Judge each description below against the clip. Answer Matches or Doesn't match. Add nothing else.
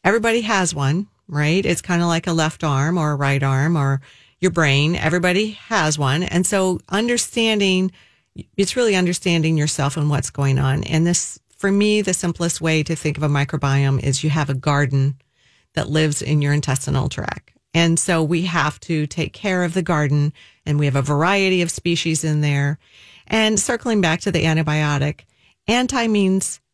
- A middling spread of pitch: Matches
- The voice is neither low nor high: Matches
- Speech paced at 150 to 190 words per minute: Matches